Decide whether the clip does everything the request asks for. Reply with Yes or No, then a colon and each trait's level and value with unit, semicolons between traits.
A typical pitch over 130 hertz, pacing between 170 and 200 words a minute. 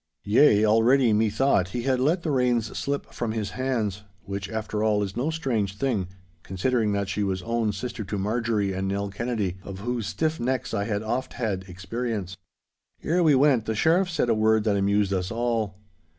No: low, 110 Hz; average, 185 wpm